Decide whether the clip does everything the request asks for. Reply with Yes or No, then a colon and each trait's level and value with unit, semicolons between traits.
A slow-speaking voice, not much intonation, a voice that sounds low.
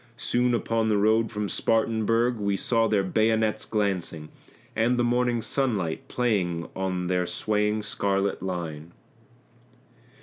No: slow, 125 wpm; average, 3.2 semitones; low, 105 Hz